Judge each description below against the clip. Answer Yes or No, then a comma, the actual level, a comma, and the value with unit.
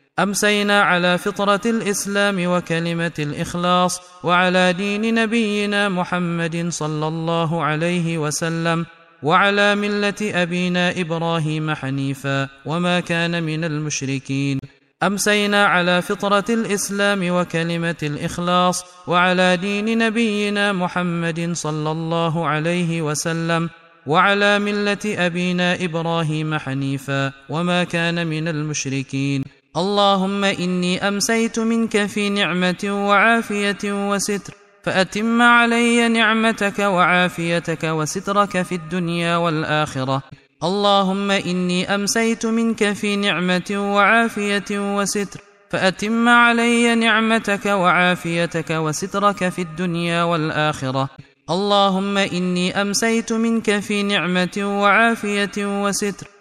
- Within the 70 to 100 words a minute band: Yes, average, 90 wpm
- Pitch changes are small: No, average, 3.4 semitones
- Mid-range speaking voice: Yes, medium, 180 Hz